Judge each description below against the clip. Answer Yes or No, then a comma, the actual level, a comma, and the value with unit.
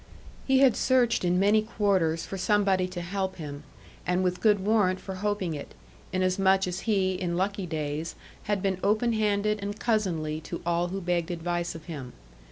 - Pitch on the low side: No, medium, 185 Hz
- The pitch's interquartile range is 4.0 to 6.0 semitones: No, average, 3.0 semitones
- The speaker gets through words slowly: No, average, 175 wpm